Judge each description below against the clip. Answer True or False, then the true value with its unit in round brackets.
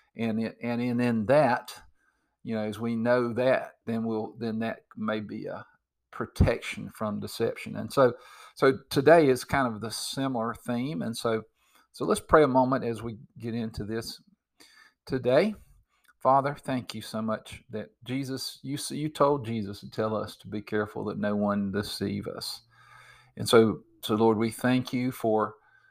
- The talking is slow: False (170 wpm)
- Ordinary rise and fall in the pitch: True (3.0 semitones)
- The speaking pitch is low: True (115 Hz)